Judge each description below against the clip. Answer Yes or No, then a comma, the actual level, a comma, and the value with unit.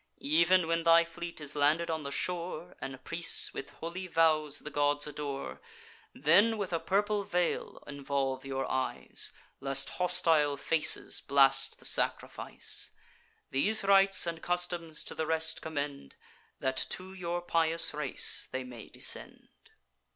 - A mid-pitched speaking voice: Yes, medium, 160 Hz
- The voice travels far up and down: No, average, 3.6 semitones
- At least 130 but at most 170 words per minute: Yes, average, 140 wpm